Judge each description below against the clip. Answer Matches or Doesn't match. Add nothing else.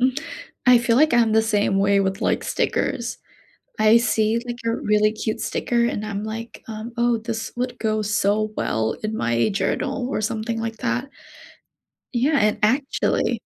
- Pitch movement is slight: Matches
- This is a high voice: Matches